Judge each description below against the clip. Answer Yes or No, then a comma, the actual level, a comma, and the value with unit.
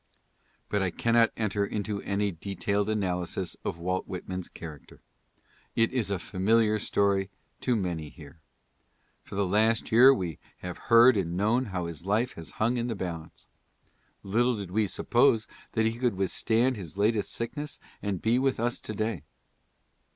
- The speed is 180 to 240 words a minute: No, average, 165 wpm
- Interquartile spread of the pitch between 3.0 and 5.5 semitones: Yes, average, 3.7 semitones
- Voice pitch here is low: Yes, low, 105 Hz